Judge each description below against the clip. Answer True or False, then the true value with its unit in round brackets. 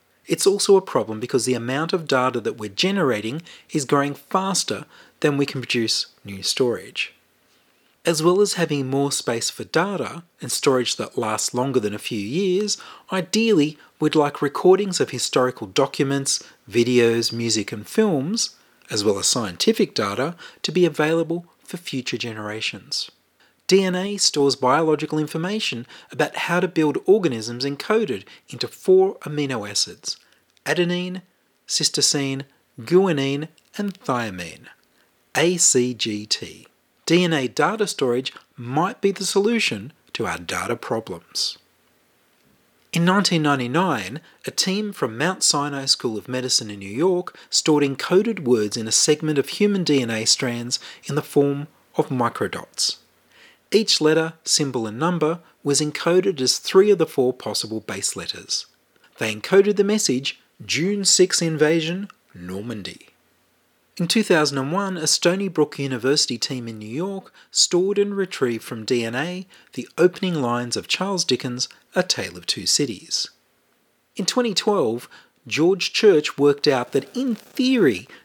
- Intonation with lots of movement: True (6.8 semitones)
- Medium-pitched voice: True (150 Hz)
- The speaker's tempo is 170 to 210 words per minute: False (140 wpm)